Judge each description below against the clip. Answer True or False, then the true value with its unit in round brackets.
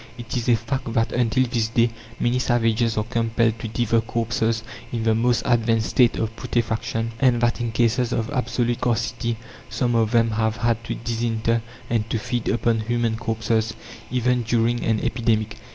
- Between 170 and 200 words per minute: True (175 wpm)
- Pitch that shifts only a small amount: True (1.1 semitones)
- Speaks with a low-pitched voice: True (115 Hz)